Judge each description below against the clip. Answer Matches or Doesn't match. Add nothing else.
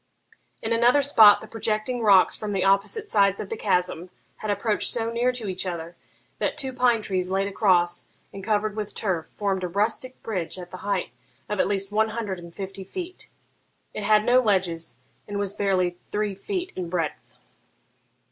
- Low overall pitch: Doesn't match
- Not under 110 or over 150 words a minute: Doesn't match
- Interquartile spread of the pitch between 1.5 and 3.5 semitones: Matches